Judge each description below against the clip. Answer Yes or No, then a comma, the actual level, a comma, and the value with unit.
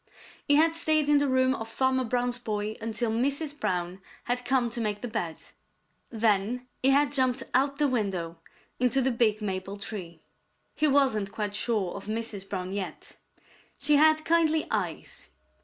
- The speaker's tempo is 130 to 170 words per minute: Yes, average, 165 wpm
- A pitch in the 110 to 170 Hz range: No, high, 240 Hz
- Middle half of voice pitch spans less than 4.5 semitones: No, average, 4.9 semitones